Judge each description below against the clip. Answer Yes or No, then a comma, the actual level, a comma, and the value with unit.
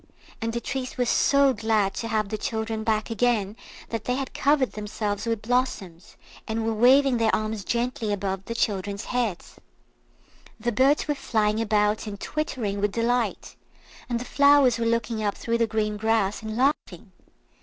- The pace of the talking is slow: No, average, 170 wpm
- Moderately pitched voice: No, high, 225 Hz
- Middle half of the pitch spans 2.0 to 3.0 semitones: Yes, average, 2.7 semitones